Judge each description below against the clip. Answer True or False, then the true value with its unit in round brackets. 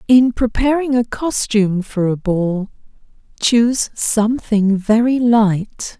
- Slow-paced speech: True (110 wpm)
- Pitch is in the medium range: False (225 Hz)